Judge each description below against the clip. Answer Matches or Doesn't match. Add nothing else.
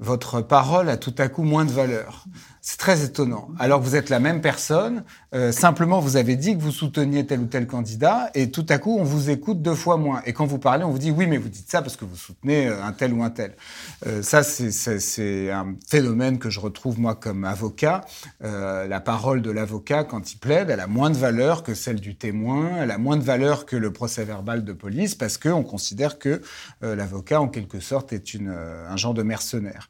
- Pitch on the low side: Matches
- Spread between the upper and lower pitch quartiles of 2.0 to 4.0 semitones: Doesn't match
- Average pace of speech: Doesn't match